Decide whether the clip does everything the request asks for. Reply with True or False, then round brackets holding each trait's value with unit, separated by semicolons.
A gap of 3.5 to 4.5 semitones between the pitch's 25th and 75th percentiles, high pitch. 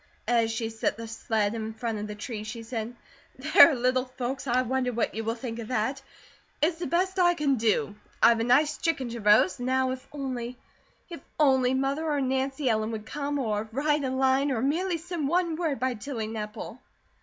True (4.0 semitones; 255 Hz)